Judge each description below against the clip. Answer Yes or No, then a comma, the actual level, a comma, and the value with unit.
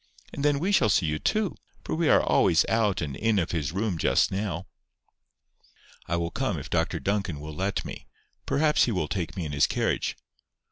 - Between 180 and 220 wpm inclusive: Yes, average, 200 wpm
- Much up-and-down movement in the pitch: Yes, wide, 5.7 semitones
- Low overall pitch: Yes, very low, 95 Hz